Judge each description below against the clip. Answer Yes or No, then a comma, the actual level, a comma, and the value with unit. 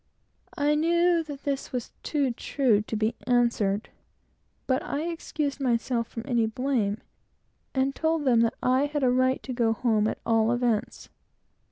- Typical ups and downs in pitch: Yes, average, 3.9 semitones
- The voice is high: Yes, very high, 255 Hz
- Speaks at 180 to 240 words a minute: No, average, 160 wpm